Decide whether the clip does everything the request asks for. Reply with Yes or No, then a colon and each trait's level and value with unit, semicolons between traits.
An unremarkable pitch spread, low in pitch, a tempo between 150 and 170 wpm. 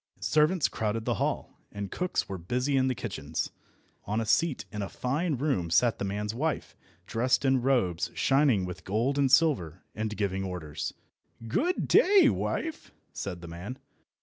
No: wide, 6.4 semitones; low, 115 Hz; average, 165 wpm